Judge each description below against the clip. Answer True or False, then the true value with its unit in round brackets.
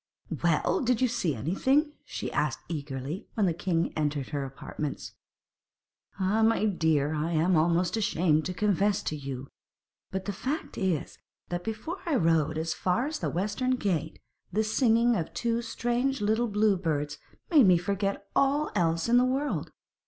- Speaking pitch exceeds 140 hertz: True (190 Hz)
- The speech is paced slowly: False (165 wpm)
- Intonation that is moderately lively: False (6.4 semitones)